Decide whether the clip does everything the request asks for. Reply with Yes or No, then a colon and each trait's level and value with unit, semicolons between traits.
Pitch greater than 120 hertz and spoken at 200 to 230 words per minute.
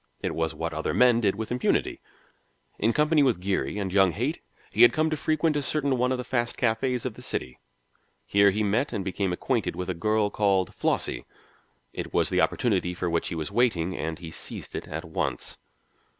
No: low, 105 Hz; fast, 205 wpm